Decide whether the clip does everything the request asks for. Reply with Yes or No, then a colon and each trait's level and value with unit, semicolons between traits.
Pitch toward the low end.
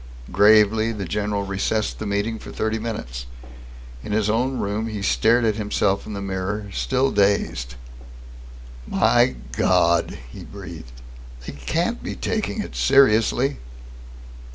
Yes: low, 105 Hz